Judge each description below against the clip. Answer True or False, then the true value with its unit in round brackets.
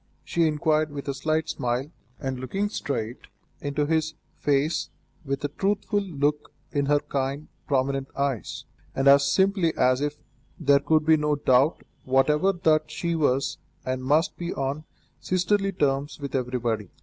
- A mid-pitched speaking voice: True (145 Hz)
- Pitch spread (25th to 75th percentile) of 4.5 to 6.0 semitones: False (2.8 semitones)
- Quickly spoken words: False (150 wpm)